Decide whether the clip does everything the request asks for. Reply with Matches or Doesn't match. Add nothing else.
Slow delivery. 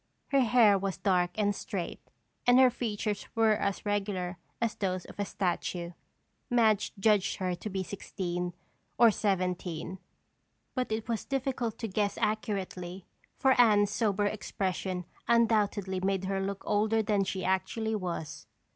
Doesn't match